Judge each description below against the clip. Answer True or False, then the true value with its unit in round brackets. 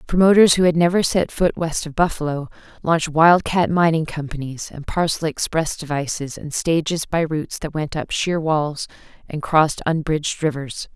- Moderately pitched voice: True (160 Hz)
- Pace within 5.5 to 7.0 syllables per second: False (5.0 syllables/s)